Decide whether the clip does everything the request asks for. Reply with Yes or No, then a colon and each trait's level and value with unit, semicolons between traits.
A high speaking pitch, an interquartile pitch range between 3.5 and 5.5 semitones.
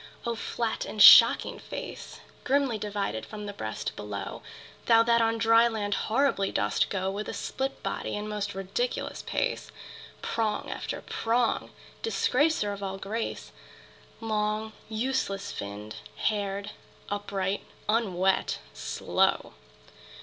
No: high, 210 Hz; average, 2.7 semitones